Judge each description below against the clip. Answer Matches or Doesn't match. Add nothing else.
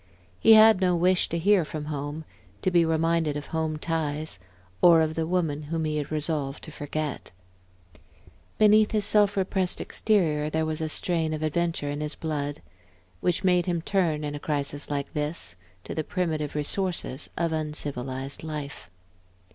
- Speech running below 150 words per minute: Doesn't match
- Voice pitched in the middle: Matches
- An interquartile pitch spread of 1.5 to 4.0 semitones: Matches